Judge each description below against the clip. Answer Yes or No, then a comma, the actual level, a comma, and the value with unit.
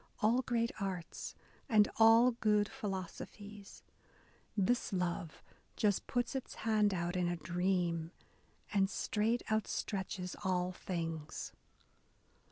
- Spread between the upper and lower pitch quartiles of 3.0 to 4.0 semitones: Yes, average, 3.6 semitones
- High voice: Yes, high, 195 Hz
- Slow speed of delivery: Yes, slow, 105 wpm